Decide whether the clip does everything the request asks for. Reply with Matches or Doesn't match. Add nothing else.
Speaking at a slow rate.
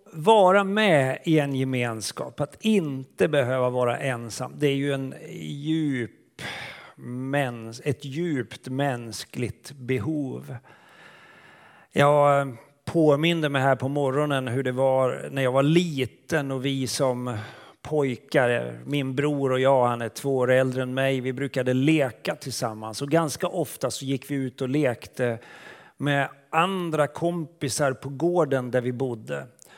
Doesn't match